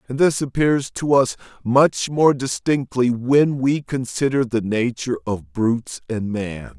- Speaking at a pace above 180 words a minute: No, average, 150 wpm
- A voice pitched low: Yes, low, 130 Hz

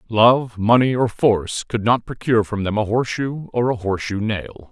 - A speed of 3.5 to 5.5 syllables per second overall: Yes, 5.2 syllables/s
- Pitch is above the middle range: No, low, 110 Hz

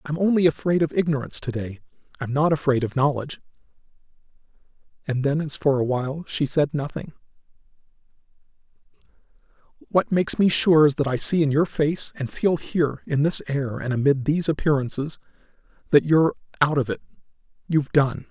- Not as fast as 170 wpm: Yes, average, 155 wpm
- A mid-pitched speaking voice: Yes, medium, 145 Hz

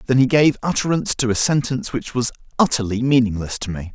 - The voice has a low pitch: Yes, low, 125 Hz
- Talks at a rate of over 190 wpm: Yes, average, 200 wpm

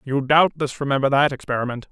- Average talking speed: Yes, average, 155 wpm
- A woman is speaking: No, male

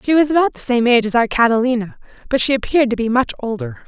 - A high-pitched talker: Yes, very high, 250 Hz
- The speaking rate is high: Yes, fast, 250 wpm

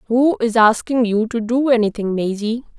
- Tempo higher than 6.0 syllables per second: No, 5.0 syllables/s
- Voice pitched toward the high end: Yes, high, 230 Hz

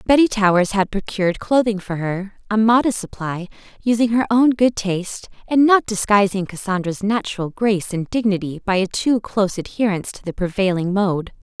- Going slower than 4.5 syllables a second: No, 5.4 syllables/s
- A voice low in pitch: No, high, 205 Hz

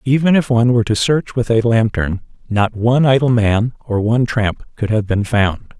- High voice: No, low, 115 Hz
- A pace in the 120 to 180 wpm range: No, fast, 205 wpm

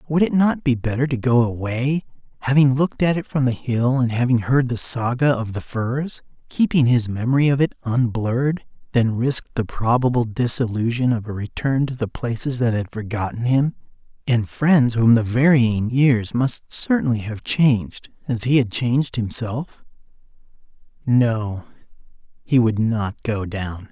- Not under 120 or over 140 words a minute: No, average, 165 wpm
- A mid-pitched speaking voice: No, low, 125 Hz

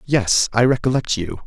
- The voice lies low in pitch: Yes, low, 120 Hz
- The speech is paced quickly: No, average, 165 wpm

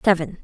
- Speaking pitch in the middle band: Yes, medium, 175 Hz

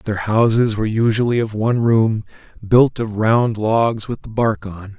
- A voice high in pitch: No, low, 110 Hz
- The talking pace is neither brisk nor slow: Yes, average, 180 wpm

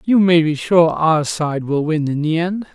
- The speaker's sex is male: Yes, male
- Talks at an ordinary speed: No, fast, 240 wpm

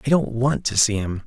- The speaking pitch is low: Yes, low, 120 Hz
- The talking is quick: Yes, fast, 285 wpm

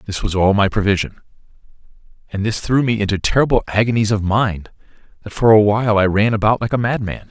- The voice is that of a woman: No, male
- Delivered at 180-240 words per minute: Yes, average, 195 wpm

